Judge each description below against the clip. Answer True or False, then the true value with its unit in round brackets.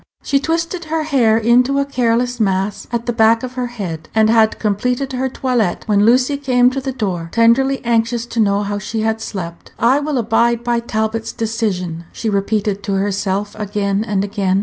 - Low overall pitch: False (225 Hz)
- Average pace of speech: True (190 wpm)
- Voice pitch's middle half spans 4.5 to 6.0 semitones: False (3.5 semitones)